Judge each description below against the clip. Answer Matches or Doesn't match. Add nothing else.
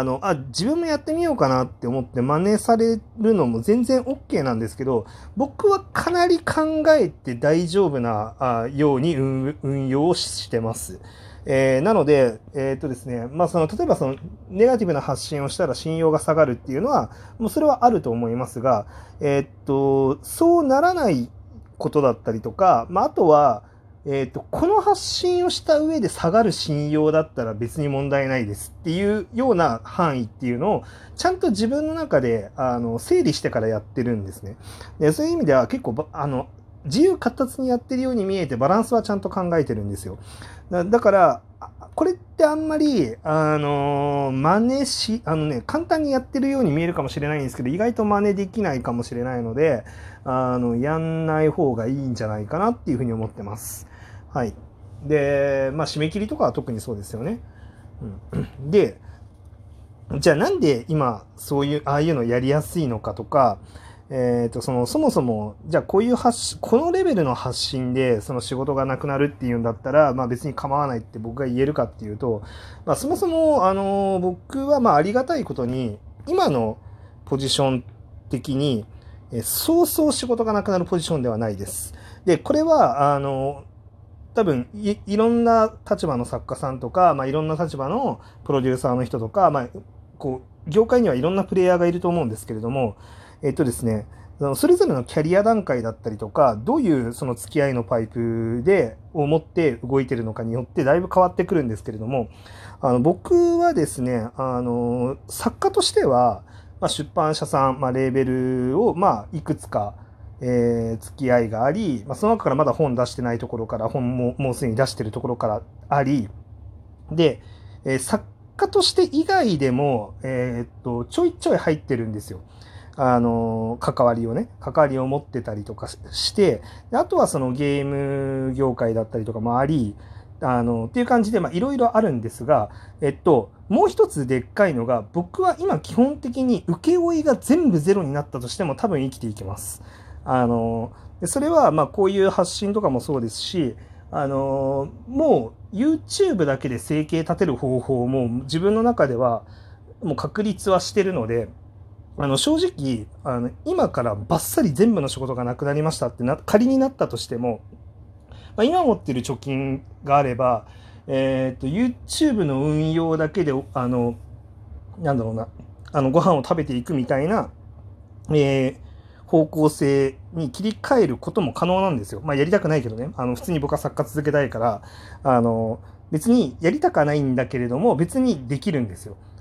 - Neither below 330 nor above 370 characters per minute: Matches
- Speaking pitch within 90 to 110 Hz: Doesn't match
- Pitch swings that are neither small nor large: Doesn't match